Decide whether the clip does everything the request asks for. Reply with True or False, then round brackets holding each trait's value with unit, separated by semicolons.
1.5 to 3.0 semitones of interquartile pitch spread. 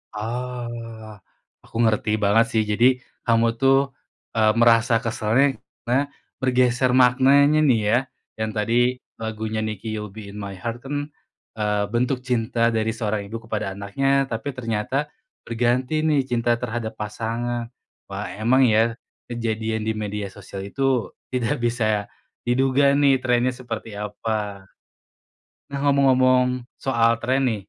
True (2.7 semitones)